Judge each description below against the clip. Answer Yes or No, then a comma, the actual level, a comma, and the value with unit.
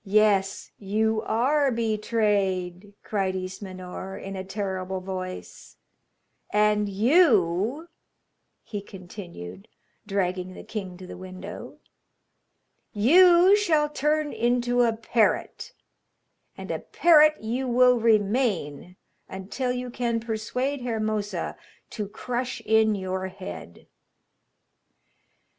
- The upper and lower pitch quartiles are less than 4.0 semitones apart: No, average, 4.6 semitones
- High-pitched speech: Yes, high, 215 Hz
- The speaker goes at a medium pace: No, slow, 100 wpm